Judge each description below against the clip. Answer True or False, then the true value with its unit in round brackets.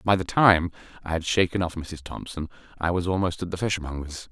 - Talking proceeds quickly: True (210 wpm)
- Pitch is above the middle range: False (85 Hz)